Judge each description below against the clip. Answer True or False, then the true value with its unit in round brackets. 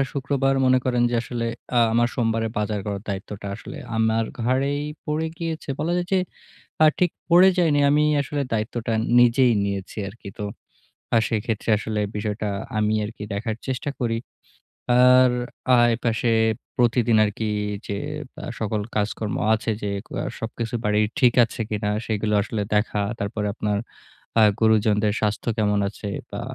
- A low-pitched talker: True (115 Hz)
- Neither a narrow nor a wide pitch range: True (3.3 semitones)